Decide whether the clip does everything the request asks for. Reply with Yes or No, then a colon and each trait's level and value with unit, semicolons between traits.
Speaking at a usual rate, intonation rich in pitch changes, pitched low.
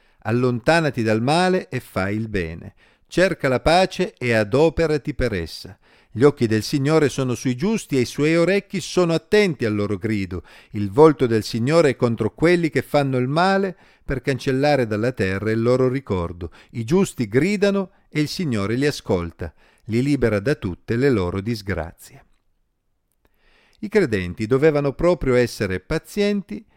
Yes: average, 155 wpm; wide, 6.6 semitones; low, 130 Hz